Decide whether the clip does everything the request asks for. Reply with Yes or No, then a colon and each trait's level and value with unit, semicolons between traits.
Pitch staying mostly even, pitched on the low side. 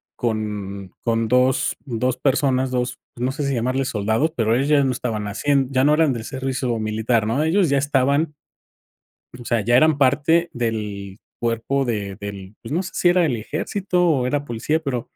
No: average, 4.3 semitones; low, 125 Hz